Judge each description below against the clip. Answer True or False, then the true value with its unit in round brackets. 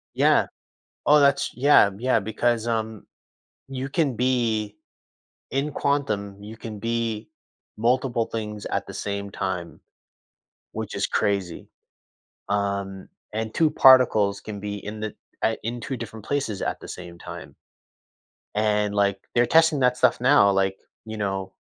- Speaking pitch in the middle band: False (110 Hz)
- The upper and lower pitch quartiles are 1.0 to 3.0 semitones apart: False (3.8 semitones)